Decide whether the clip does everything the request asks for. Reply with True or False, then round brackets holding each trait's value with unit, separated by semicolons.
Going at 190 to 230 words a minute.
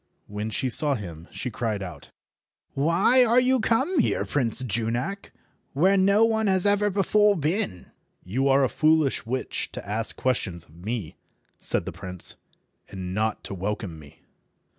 False (160 wpm)